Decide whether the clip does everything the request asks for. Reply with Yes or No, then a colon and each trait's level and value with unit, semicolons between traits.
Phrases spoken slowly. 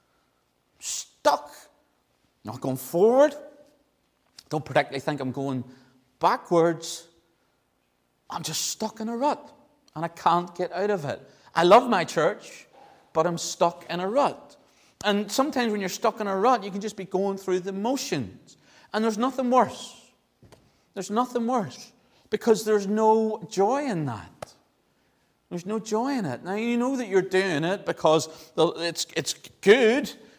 No: average, 155 wpm